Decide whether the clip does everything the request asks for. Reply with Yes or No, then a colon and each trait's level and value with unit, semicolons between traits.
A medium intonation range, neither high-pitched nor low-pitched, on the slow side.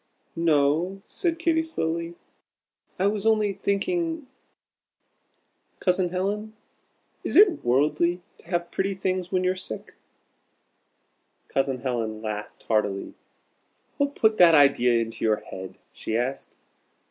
No: wide, 8.1 semitones; medium, 180 Hz; slow, 115 wpm